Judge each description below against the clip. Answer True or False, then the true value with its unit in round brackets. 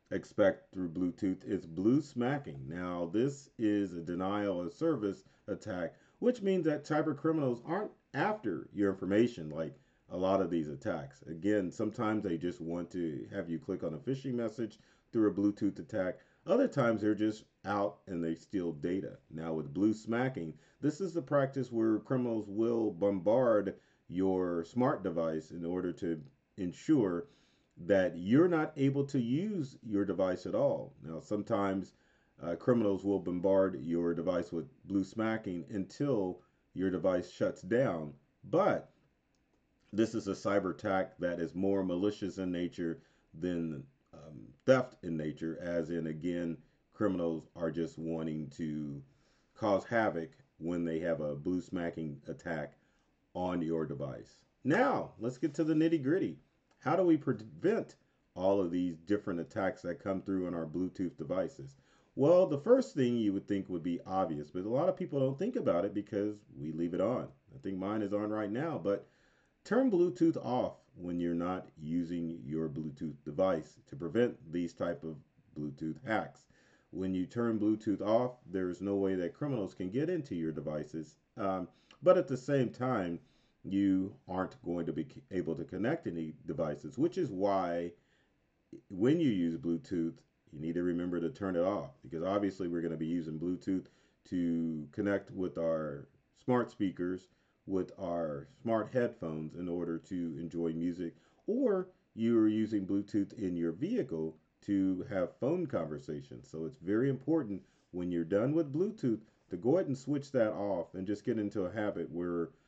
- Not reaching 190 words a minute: True (165 wpm)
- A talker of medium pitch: False (95 Hz)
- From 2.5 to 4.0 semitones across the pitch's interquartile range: False (5.2 semitones)